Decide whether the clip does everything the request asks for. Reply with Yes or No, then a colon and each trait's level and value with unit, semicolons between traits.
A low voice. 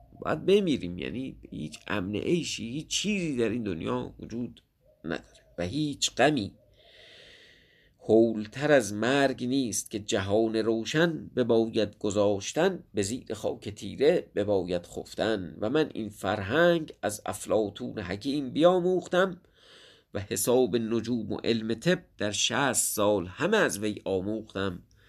Yes: low, 115 Hz